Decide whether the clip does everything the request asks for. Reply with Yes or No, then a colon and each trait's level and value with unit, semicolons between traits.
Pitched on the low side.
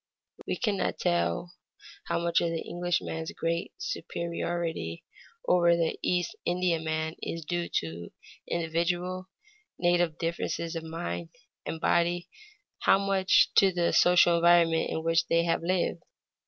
No: medium, 170 Hz